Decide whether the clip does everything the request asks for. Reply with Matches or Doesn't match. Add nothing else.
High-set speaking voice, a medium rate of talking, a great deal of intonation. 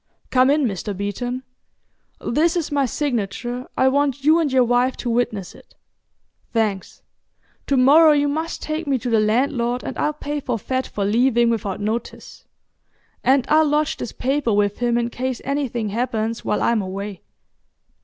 Doesn't match